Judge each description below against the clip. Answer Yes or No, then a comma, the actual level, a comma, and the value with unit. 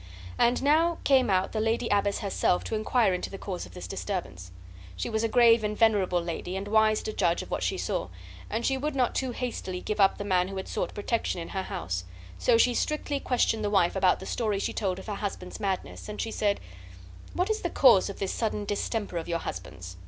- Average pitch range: Yes, average, 3.7 semitones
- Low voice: No, high, 205 Hz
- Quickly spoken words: Yes, fast, 230 wpm